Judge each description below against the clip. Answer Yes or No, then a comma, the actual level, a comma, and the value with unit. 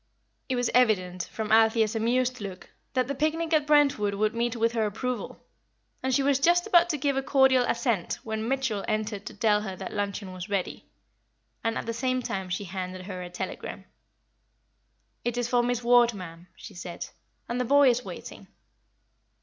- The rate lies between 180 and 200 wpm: Yes, average, 185 wpm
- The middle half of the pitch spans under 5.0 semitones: Yes, average, 4.0 semitones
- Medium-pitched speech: No, high, 230 Hz